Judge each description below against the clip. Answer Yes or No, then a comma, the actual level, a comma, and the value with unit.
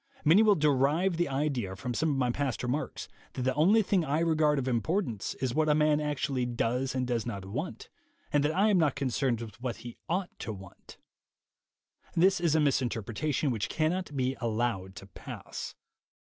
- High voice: No, low, 135 Hz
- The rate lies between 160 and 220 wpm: Yes, average, 190 wpm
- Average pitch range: Yes, average, 4.5 semitones